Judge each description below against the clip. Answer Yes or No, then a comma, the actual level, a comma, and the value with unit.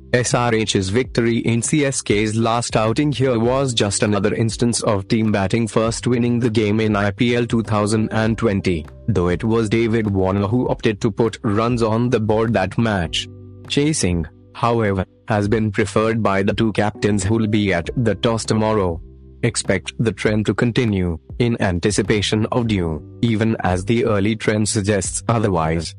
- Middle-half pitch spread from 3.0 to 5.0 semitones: No, narrow, 2.6 semitones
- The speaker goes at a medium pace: Yes, average, 155 wpm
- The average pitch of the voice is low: Yes, low, 110 Hz